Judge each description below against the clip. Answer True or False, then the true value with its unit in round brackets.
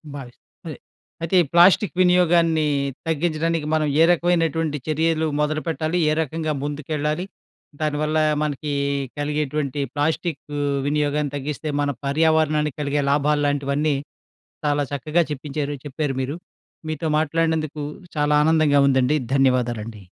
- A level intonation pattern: True (1.8 semitones)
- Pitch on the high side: False (150 Hz)